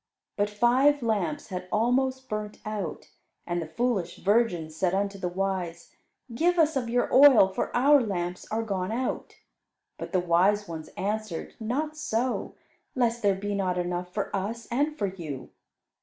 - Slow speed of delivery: No, average, 160 wpm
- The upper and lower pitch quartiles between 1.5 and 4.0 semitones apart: No, average, 4.9 semitones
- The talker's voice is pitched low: No, high, 205 Hz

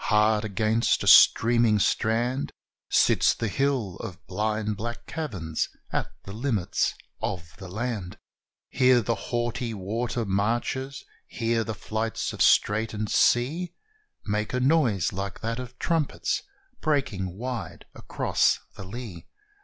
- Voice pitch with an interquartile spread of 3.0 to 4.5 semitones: Yes, average, 3.3 semitones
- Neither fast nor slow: No, slow, 125 wpm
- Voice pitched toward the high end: No, low, 115 Hz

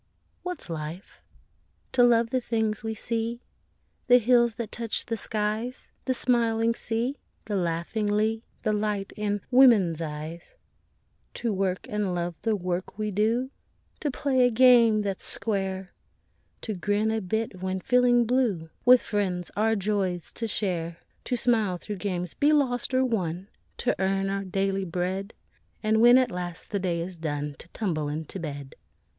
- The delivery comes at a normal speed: Yes, average, 160 wpm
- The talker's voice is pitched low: No, high, 210 Hz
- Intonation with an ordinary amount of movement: Yes, average, 4.2 semitones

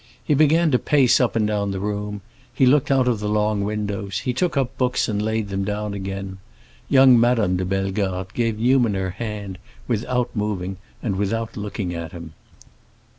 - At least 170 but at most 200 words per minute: Yes, average, 180 wpm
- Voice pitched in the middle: No, low, 105 Hz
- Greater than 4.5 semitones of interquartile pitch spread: No, average, 3.9 semitones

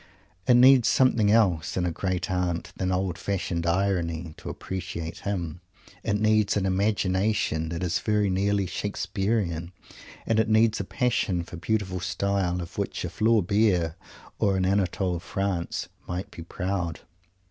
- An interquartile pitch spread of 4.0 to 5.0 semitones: No, average, 2.9 semitones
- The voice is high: No, very low, 95 Hz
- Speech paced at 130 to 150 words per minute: Yes, average, 145 wpm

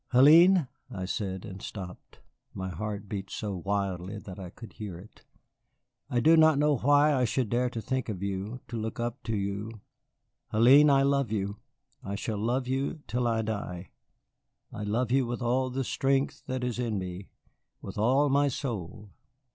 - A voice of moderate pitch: No, low, 115 Hz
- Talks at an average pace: Yes, average, 180 wpm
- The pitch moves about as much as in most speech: Yes, average, 4.6 semitones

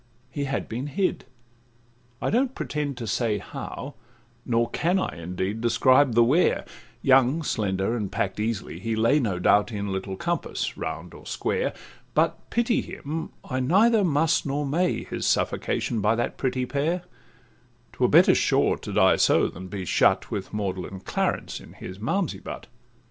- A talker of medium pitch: No, low, 120 Hz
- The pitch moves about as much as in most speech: No, wide, 6.0 semitones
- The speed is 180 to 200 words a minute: No, average, 160 wpm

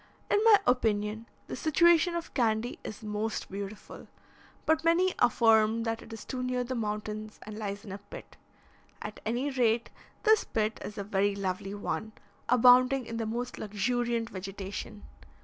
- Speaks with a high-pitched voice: Yes, high, 225 Hz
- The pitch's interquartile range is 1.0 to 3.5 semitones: Yes, average, 3.1 semitones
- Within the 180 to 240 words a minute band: No, average, 160 wpm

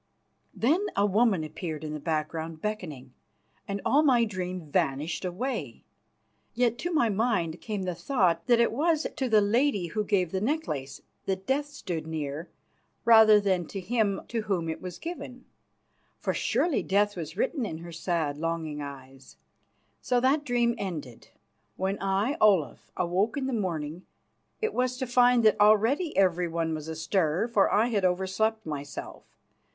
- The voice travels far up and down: Yes, wide, 6.4 semitones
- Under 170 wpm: Yes, average, 160 wpm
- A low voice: No, high, 195 Hz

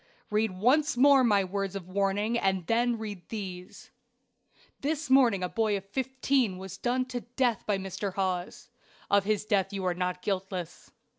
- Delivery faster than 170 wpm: No, average, 165 wpm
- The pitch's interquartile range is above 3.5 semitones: Yes, average, 4.2 semitones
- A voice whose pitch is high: Yes, high, 200 Hz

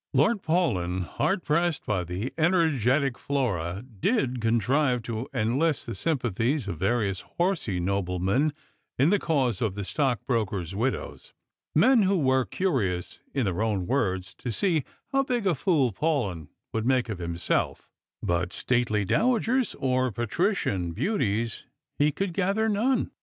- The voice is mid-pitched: No, low, 125 Hz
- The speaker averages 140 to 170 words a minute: Yes, average, 150 wpm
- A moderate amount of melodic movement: No, wide, 8.5 semitones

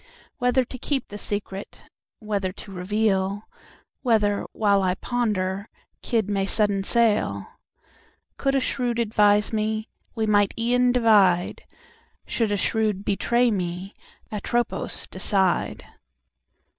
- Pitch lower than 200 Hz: No, high, 210 Hz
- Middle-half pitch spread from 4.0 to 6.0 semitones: No, average, 3.1 semitones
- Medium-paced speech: No, slow, 90 wpm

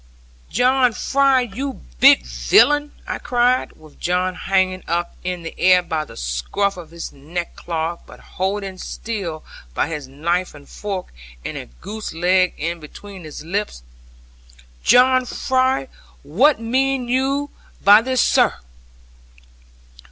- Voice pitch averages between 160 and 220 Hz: Yes, medium, 185 Hz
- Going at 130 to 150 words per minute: Yes, slow, 135 wpm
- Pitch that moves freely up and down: Yes, wide, 7.2 semitones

